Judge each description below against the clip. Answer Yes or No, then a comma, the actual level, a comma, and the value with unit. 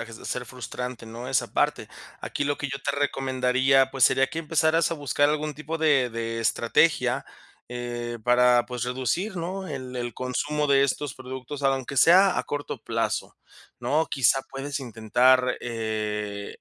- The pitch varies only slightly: No, average, 3.0 semitones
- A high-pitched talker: No, low, 130 Hz